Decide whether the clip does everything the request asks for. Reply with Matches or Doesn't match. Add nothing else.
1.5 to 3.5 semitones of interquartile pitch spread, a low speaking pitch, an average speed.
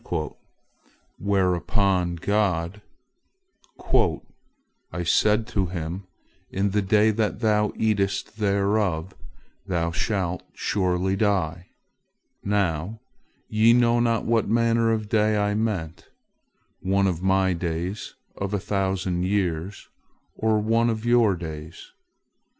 Doesn't match